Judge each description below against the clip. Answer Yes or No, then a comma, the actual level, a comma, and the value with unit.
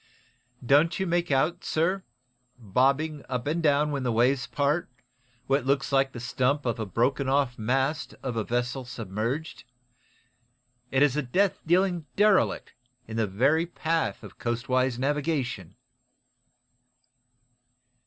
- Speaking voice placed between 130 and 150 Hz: Yes, low, 135 Hz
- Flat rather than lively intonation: No, average, 4.1 semitones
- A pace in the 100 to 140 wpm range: Yes, slow, 135 wpm